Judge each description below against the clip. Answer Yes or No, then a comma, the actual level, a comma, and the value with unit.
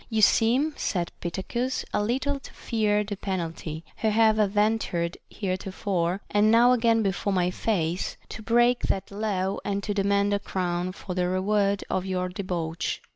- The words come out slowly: No, average, 165 wpm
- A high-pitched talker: Yes, high, 200 Hz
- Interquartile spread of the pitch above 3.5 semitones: No, average, 3.1 semitones